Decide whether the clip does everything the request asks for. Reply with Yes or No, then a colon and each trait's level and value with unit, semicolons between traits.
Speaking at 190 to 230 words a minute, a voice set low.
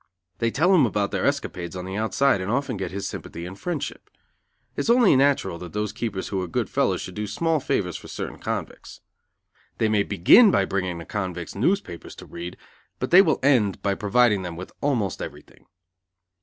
Yes: average, 195 wpm; low, 105 Hz